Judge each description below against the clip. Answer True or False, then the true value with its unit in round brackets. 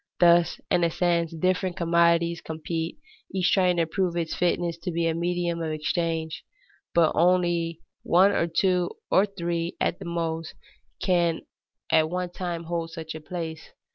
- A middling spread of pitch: False (1.2 semitones)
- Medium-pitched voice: True (170 Hz)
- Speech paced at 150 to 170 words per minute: True (160 wpm)